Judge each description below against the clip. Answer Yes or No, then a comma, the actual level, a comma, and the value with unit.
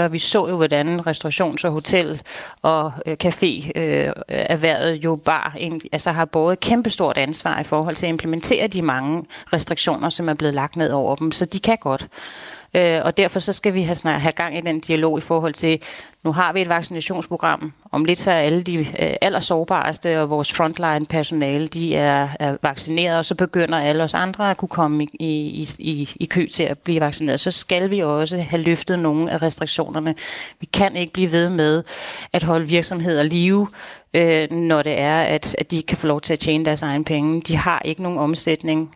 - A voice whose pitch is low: No, medium, 165 Hz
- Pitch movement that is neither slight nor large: No, narrow, 2.0 semitones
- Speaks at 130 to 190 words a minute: No, average, 200 wpm